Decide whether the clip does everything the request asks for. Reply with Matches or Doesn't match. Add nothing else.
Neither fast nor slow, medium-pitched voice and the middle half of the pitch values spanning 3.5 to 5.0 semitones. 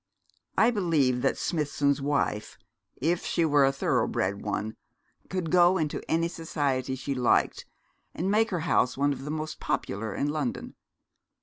Matches